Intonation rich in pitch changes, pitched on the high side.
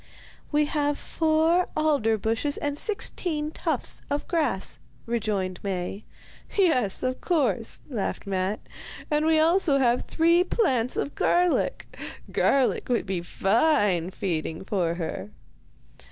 Yes: wide, 8.0 semitones; very high, 255 Hz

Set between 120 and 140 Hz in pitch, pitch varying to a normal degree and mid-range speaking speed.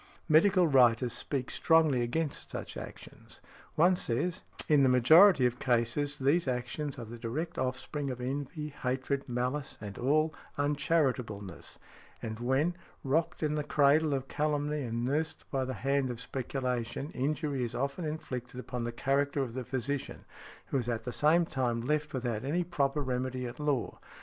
Yes: low, 135 Hz; average, 3.3 semitones; average, 160 wpm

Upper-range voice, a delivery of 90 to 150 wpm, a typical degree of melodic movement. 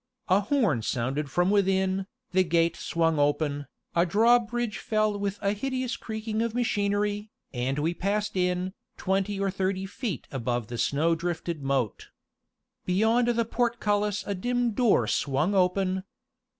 Yes: high, 195 Hz; average, 140 wpm; average, 4.4 semitones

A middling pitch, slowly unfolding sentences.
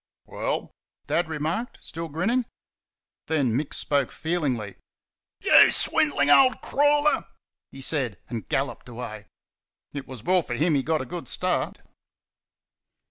Yes: medium, 150 Hz; slow, 130 wpm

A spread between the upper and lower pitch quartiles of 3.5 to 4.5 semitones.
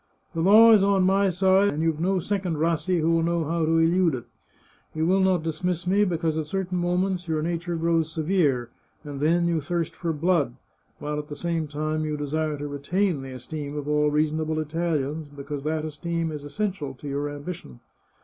No: average, 3.0 semitones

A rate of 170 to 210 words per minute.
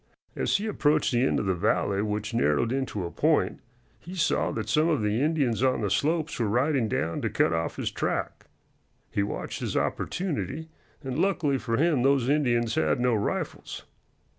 Yes: average, 185 wpm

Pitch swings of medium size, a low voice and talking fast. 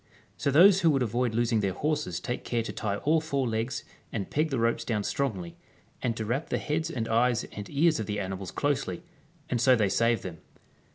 Yes: average, 4.7 semitones; low, 120 Hz; fast, 215 wpm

